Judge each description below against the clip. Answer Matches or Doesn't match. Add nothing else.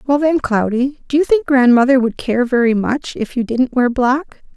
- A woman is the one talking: Matches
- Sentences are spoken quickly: Matches